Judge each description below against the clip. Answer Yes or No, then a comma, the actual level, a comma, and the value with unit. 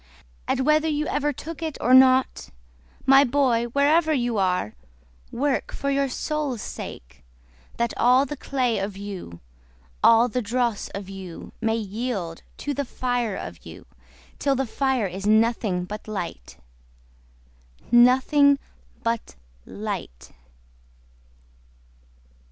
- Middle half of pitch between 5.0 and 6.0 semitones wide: Yes, wide, 5.4 semitones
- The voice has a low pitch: No, high, 240 Hz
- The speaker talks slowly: Yes, slow, 125 wpm